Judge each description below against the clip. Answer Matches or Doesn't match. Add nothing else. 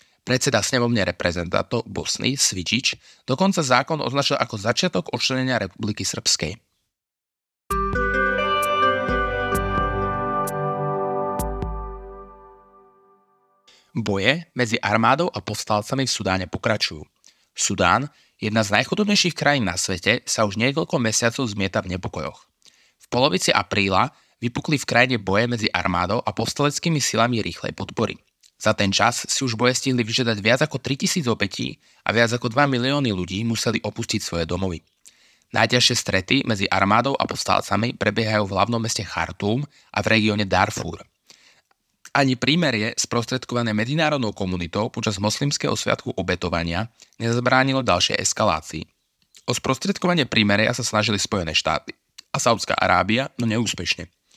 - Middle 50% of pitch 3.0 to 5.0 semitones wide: Matches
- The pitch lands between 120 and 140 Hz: Doesn't match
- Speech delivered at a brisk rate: Doesn't match